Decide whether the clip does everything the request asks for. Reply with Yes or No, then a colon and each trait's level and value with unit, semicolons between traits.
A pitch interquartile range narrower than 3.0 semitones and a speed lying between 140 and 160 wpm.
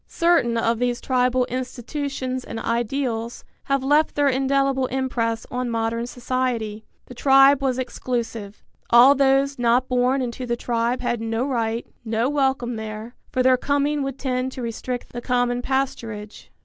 Yes: narrow, 2.4 semitones; average, 150 wpm